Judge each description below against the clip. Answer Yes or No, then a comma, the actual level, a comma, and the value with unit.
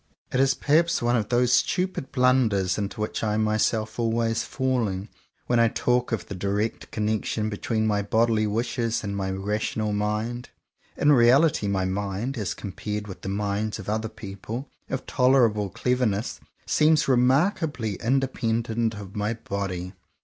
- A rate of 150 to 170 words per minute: Yes, average, 155 wpm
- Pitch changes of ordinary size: Yes, average, 3.3 semitones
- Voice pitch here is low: Yes, low, 110 Hz